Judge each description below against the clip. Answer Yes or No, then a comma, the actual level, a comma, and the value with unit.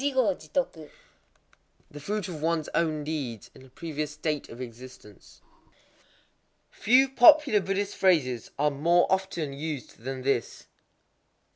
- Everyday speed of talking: No, slow, 120 wpm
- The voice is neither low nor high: Yes, medium, 155 Hz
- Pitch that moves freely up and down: Yes, wide, 5.8 semitones